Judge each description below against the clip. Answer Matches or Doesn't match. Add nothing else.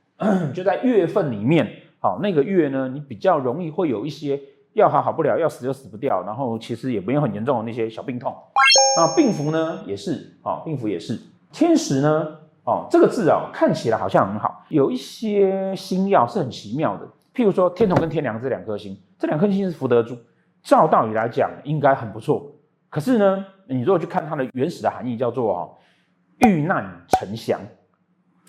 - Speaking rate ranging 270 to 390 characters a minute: Matches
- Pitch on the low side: Doesn't match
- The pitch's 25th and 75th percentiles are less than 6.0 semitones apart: Doesn't match